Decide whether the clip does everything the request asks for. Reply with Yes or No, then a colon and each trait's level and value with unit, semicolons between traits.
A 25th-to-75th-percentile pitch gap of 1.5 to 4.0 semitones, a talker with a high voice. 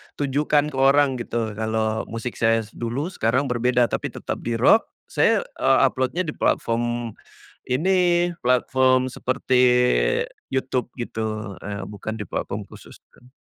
No: average, 3.1 semitones; low, 125 Hz